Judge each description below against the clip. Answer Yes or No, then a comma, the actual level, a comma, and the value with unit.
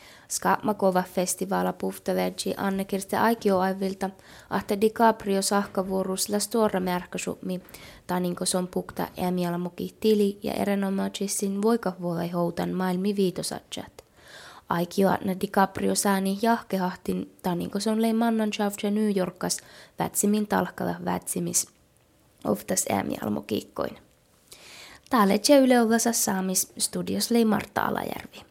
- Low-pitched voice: No, high, 195 Hz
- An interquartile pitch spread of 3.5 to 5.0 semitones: No, narrow, 2.4 semitones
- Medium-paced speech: No, slow, 85 wpm